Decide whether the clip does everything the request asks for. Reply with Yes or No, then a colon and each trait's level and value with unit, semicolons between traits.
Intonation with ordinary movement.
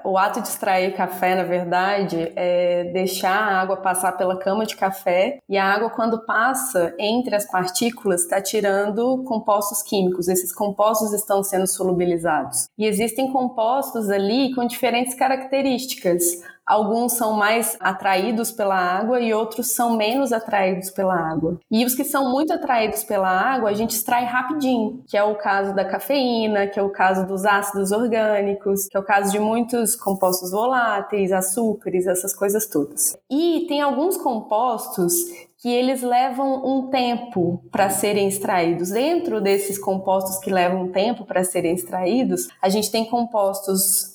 Yes: average, 4.0 semitones